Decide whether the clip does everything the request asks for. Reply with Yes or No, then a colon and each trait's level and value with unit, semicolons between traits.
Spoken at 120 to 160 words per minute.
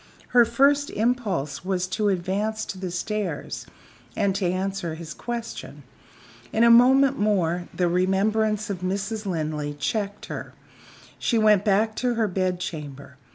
Yes: average, 145 wpm